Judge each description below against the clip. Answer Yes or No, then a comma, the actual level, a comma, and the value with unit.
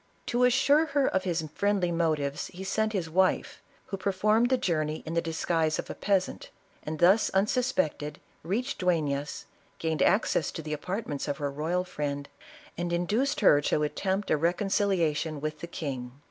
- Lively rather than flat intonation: No, average, 4.6 semitones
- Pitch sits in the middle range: Yes, medium, 170 Hz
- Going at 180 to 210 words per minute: No, average, 170 wpm